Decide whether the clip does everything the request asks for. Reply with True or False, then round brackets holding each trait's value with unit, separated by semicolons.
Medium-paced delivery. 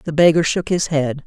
False (235 wpm)